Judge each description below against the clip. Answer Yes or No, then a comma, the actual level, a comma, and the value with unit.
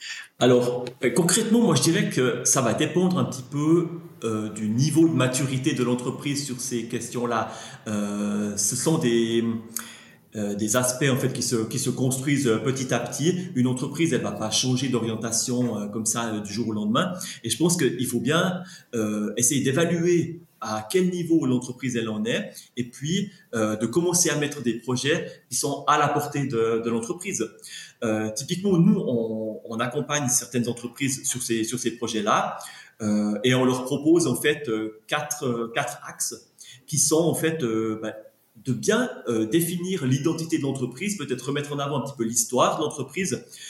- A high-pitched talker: No, low, 125 Hz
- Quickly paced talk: No, average, 185 wpm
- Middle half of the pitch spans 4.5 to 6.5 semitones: Yes, average, 5.3 semitones